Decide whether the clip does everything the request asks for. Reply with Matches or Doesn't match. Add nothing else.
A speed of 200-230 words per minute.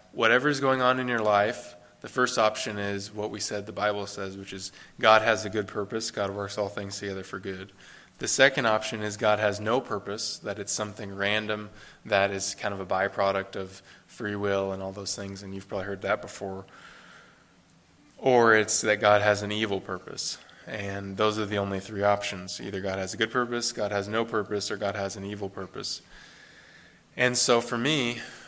Matches